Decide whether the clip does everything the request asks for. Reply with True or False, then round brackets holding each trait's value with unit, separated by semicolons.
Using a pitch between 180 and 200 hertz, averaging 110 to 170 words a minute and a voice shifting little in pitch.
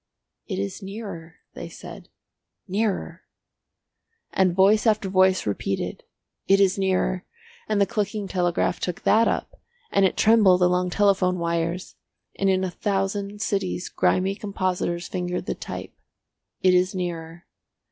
True (185 Hz; 135 wpm; 1.9 semitones)